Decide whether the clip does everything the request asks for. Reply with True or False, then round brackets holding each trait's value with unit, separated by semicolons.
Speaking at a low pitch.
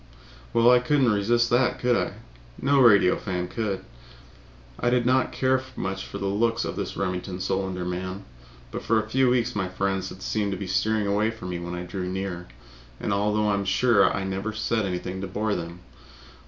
True (100 Hz)